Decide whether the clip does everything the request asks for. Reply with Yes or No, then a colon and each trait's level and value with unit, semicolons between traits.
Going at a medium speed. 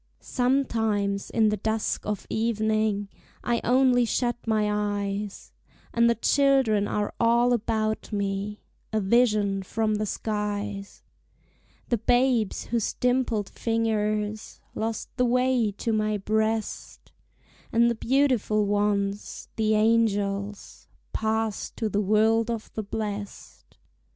No: slow, 115 wpm